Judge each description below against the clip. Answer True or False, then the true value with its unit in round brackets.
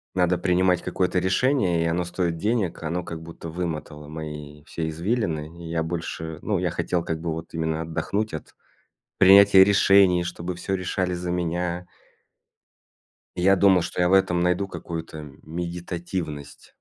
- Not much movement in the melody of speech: True (2.1 semitones)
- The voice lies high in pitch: False (85 Hz)